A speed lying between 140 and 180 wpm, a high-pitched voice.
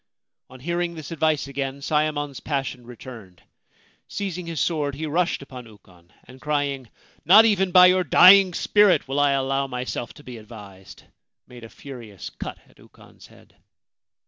No: average, 160 wpm; medium, 140 Hz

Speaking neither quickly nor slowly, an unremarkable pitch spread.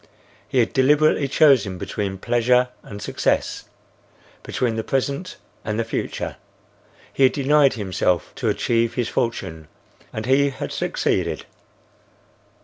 No: slow, 120 wpm; average, 4.0 semitones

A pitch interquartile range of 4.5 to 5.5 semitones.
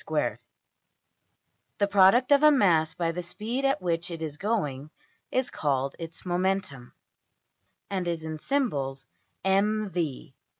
Yes: average, 5.0 semitones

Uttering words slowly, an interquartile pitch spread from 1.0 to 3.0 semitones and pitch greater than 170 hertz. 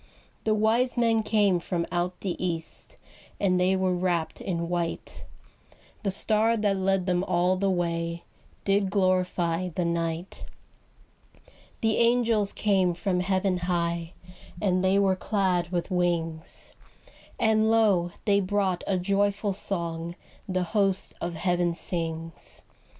Yes: slow, 130 wpm; narrow, 2.6 semitones; medium, 185 Hz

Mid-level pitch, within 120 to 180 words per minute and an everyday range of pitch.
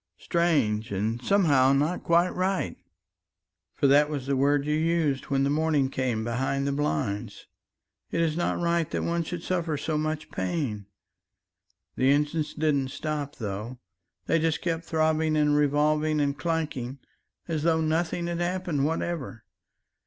Yes: medium, 150 Hz; average, 150 wpm; average, 3.2 semitones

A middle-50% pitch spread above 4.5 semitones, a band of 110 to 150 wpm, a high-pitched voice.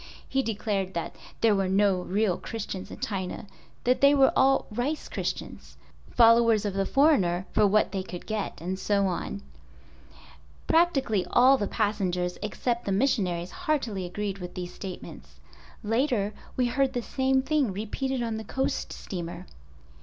Yes: average, 5.1 semitones; average, 145 wpm; high, 210 Hz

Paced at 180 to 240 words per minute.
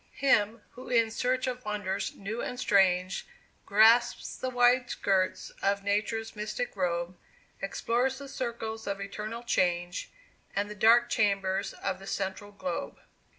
No: average, 140 wpm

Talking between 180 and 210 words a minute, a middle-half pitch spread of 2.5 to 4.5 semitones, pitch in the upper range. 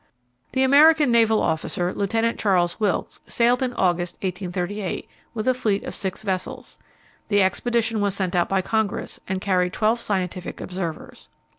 No: average, 150 wpm; average, 4.0 semitones; high, 200 Hz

